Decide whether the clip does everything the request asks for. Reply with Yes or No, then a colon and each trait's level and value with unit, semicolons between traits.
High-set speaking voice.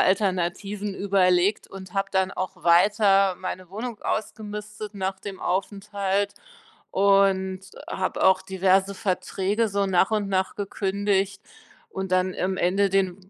Yes: high, 195 Hz